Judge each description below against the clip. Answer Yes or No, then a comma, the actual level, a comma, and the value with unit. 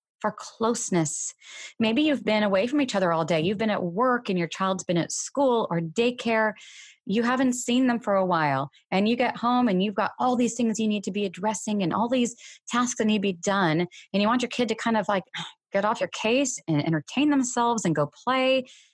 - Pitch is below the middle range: No, high, 220 Hz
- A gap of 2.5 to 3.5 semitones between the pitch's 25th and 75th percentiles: No, average, 4.2 semitones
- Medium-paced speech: No, fast, 230 wpm